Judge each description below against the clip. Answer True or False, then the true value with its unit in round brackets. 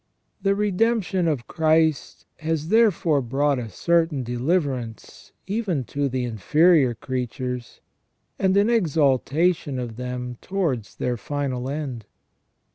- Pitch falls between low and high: True (145 Hz)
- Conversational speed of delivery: False (120 wpm)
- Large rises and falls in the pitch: True (5.7 semitones)